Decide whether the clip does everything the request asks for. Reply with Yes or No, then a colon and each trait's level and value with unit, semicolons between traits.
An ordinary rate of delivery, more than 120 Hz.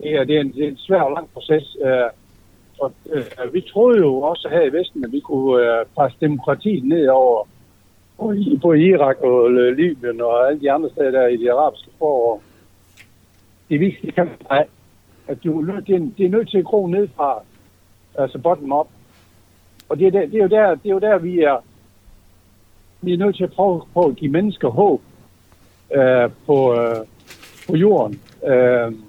Yes: average, 190 wpm; low, 135 Hz